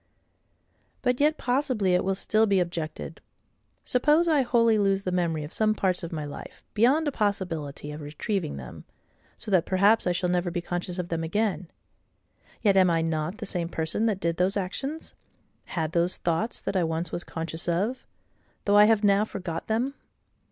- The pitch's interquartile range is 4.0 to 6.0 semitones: Yes, average, 4.5 semitones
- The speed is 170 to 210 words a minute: Yes, average, 180 wpm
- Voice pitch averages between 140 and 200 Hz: Yes, medium, 185 Hz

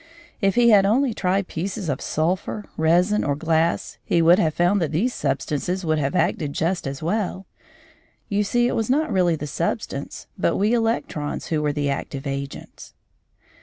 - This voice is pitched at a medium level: Yes, medium, 175 Hz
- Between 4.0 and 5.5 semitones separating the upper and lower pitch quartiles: Yes, average, 5.2 semitones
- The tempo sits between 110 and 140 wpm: No, average, 175 wpm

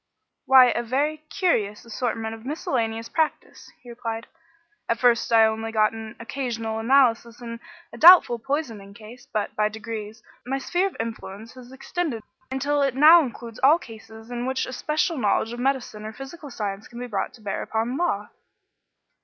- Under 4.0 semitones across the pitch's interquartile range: Yes, average, 3.4 semitones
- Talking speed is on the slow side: No, average, 170 wpm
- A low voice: No, high, 235 Hz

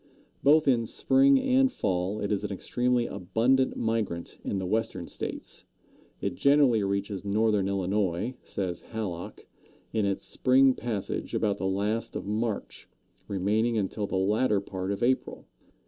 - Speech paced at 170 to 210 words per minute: No, average, 145 wpm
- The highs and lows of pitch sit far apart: No, average, 3.6 semitones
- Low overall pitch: Yes, low, 105 Hz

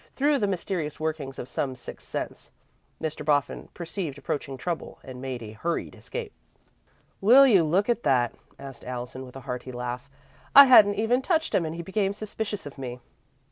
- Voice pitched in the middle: Yes, medium, 155 Hz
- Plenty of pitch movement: Yes, wide, 7.6 semitones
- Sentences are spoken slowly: No, average, 180 wpm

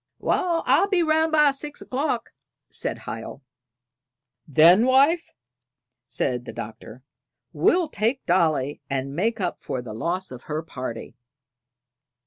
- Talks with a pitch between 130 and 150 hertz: No, medium, 185 Hz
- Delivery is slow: Yes, slow, 125 wpm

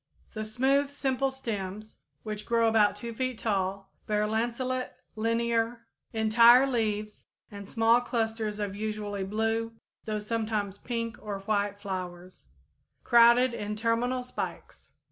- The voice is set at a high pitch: Yes, high, 220 Hz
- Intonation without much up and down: Yes, narrow, 2.2 semitones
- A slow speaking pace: Yes, slow, 125 wpm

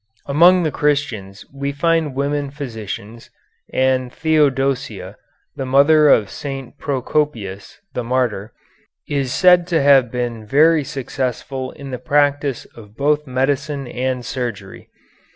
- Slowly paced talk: Yes, slow, 120 wpm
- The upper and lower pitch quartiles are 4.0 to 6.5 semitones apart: No, average, 3.0 semitones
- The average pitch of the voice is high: No, low, 135 Hz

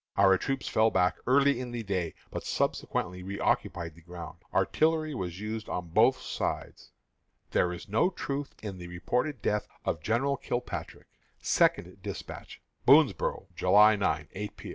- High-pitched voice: No, low, 105 Hz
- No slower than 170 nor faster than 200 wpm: No, average, 150 wpm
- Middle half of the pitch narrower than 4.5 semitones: No, wide, 5.6 semitones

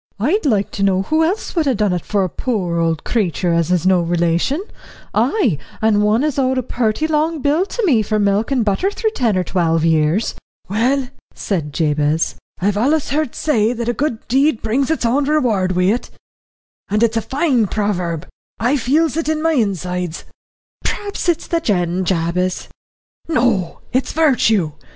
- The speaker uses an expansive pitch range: Yes, wide, 7.6 semitones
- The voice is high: Yes, high, 220 Hz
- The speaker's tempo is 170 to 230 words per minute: Yes, average, 180 wpm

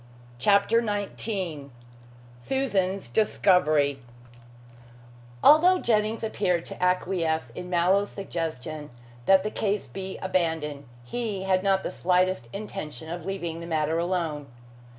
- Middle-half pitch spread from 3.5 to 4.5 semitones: Yes, average, 3.8 semitones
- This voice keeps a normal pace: No, slow, 115 wpm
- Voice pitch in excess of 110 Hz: Yes, medium, 185 Hz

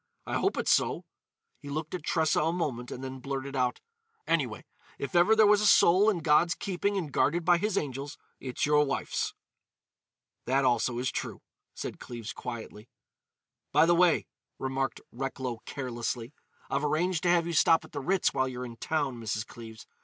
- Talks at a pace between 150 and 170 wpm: No, average, 180 wpm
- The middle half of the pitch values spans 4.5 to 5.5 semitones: Yes, average, 5.2 semitones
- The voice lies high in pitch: No, medium, 140 Hz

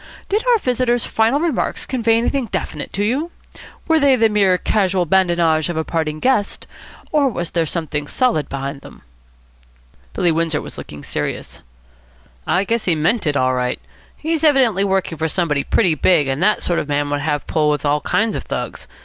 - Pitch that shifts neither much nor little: No, wide, 7.3 semitones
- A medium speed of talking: Yes, average, 190 wpm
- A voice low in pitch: No, medium, 180 Hz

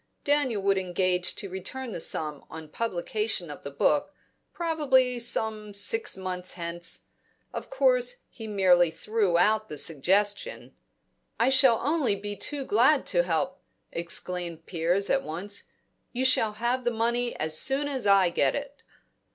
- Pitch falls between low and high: No, high, 205 Hz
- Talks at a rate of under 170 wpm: Yes, average, 150 wpm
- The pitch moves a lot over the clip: Yes, wide, 6.4 semitones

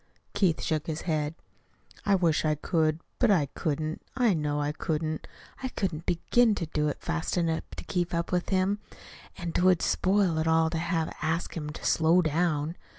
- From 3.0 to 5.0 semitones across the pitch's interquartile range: No, narrow, 2.5 semitones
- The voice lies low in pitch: No, medium, 165 Hz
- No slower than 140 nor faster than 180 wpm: No, average, 195 wpm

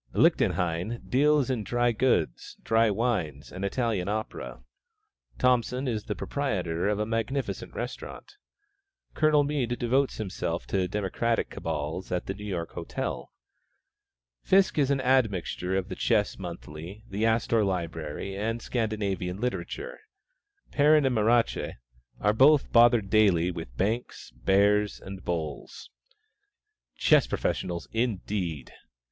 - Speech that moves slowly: Yes, slow, 120 wpm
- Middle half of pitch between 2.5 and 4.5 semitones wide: No, average, 5.1 semitones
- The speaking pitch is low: Yes, low, 105 Hz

